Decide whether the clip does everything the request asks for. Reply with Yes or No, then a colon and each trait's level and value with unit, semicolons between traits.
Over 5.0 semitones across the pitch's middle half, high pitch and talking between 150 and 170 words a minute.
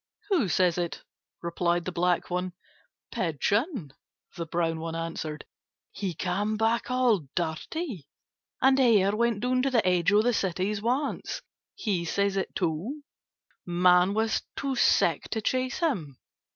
No: wide, 5.5 semitones; high, 195 Hz; average, 140 wpm